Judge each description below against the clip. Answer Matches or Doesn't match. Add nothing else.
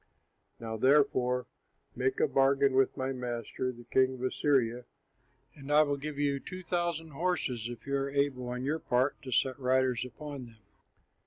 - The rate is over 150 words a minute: Matches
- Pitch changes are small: Matches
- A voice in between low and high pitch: Doesn't match